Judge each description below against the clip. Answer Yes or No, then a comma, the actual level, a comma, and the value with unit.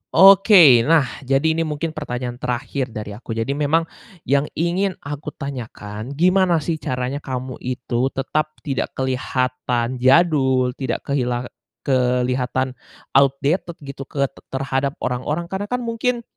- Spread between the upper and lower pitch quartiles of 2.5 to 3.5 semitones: No, average, 4.1 semitones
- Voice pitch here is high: No, low, 135 Hz